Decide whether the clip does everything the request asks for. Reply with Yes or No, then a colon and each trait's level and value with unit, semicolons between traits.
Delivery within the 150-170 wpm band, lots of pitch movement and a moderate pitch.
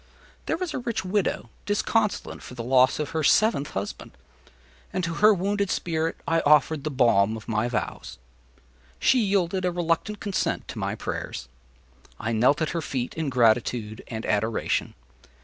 Yes: average, 165 wpm; wide, 8.1 semitones; medium, 155 Hz